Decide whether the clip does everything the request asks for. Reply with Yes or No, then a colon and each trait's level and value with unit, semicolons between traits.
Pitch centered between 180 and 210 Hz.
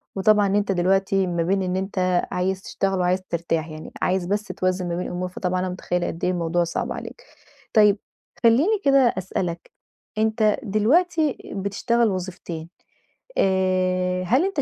Yes: high, 190 Hz